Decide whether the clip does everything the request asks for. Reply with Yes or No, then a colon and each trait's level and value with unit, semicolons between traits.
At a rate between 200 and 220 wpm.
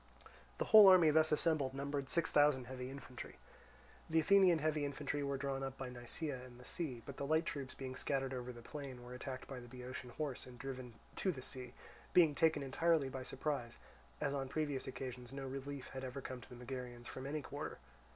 Yes: fast, 205 wpm